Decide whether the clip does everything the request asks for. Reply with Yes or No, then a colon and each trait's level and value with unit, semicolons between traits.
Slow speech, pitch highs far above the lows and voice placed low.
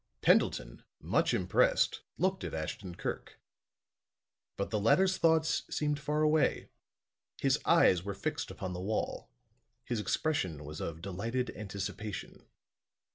Yes: slow, 125 wpm; wide, 8.6 semitones; low, 105 Hz